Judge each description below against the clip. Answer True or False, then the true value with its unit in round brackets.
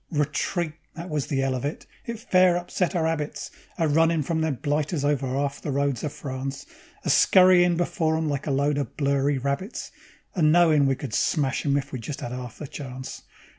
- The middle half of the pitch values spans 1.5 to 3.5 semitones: True (3.0 semitones)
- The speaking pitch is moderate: True (145 Hz)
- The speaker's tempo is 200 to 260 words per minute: True (205 wpm)